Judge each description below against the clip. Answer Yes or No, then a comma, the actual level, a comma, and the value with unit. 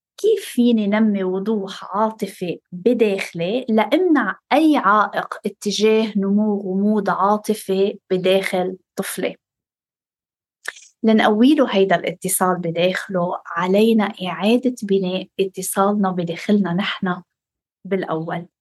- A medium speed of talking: No, slow, 85 wpm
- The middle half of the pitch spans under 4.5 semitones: Yes, average, 2.8 semitones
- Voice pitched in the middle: No, high, 195 Hz